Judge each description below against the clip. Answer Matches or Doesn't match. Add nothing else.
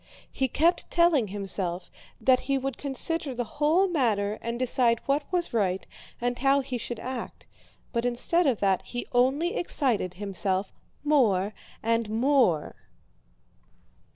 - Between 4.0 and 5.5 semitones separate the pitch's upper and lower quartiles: Matches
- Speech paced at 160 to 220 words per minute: Doesn't match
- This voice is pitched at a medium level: Doesn't match